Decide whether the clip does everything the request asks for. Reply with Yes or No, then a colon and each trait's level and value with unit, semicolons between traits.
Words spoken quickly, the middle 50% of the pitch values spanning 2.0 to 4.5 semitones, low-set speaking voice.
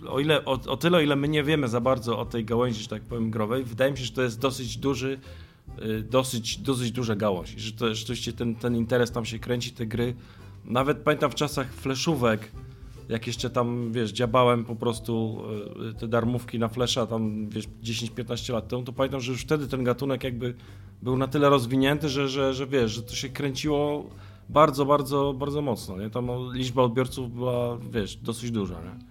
Yes: fast, 210 wpm; average, 2.7 semitones; low, 120 Hz